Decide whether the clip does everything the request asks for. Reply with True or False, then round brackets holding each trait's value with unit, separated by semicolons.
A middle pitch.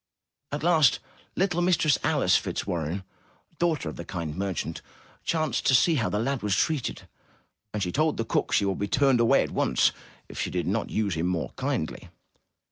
False (115 Hz)